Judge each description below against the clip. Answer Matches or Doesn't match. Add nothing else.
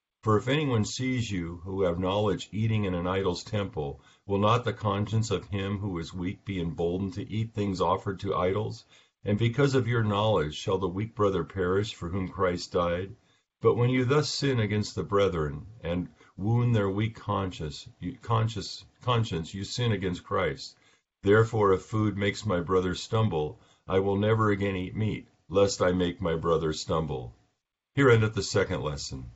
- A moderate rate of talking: Matches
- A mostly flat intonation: Doesn't match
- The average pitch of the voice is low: Matches